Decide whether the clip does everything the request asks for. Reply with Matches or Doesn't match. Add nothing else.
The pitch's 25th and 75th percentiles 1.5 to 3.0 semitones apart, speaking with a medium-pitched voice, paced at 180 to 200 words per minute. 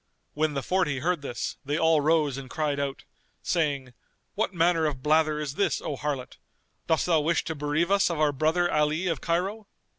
Matches